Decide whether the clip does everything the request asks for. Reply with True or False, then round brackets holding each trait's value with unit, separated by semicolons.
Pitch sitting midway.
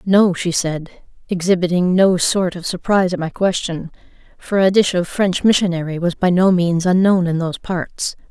True (180 Hz)